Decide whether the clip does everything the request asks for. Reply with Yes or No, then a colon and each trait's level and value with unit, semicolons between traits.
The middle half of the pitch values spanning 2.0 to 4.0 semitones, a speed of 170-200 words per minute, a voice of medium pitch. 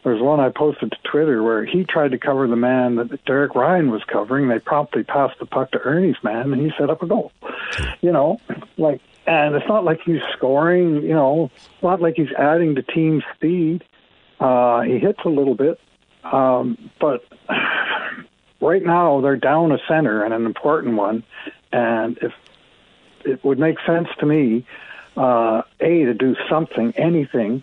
No: average, 4.4 semitones; average, 180 wpm; medium, 145 Hz